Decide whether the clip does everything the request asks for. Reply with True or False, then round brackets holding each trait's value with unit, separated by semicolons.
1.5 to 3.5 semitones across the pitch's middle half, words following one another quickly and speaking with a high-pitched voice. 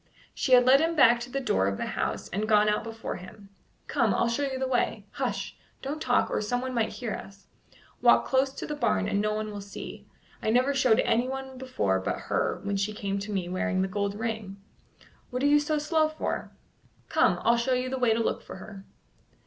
False (4.5 semitones; 220 wpm; 230 Hz)